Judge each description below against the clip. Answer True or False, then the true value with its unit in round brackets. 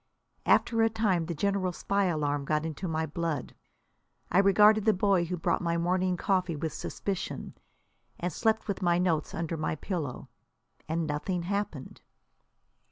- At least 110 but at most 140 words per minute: False (155 wpm)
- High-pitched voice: False (175 Hz)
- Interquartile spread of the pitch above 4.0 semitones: False (3.6 semitones)